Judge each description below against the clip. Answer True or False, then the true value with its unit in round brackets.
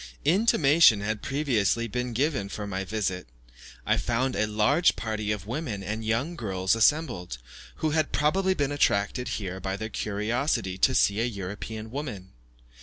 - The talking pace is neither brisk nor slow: True (155 wpm)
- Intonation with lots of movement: True (5.9 semitones)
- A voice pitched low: True (110 Hz)